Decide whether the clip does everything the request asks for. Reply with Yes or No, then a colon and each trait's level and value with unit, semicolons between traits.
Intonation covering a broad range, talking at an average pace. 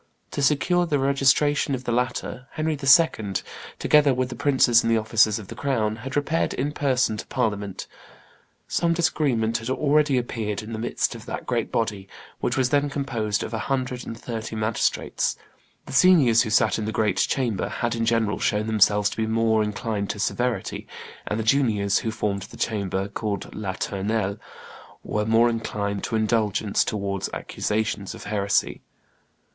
No: average, 3.9 semitones; average, 170 wpm